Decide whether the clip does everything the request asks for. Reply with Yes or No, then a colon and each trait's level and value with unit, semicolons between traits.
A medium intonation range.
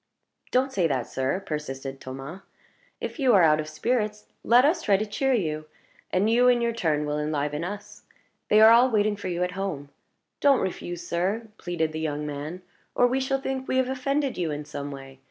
No: wide, 8.0 semitones